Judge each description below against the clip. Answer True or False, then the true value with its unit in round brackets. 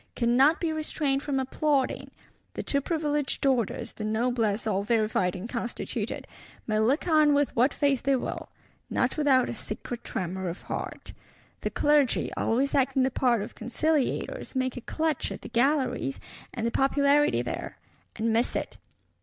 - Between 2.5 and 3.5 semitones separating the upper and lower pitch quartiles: False (4.1 semitones)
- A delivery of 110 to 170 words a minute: True (160 wpm)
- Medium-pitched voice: False (260 Hz)